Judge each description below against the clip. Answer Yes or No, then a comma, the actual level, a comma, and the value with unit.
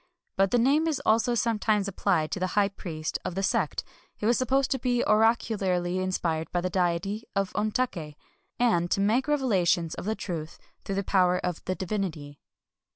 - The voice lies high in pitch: Yes, high, 195 Hz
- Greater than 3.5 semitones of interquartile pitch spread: Yes, average, 4.4 semitones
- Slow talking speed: No, average, 175 wpm